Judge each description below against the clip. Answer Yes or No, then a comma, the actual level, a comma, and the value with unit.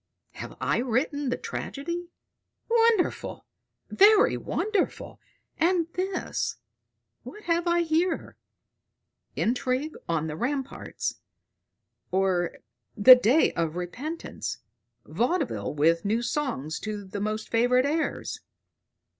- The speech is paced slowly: Yes, slow, 100 wpm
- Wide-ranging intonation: Yes, wide, 8.6 semitones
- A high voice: Yes, very high, 260 Hz